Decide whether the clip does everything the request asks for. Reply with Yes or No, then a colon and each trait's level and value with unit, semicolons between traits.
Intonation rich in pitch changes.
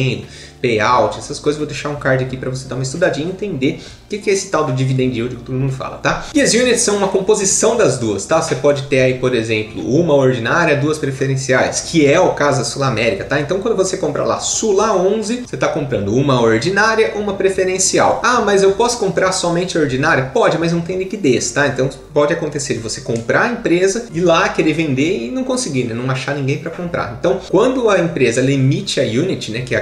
Yes: wide, 6.5 semitones